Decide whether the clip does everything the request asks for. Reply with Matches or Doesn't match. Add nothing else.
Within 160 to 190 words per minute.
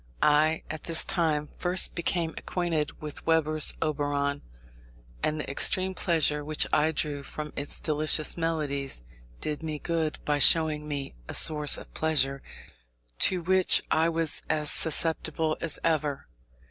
Doesn't match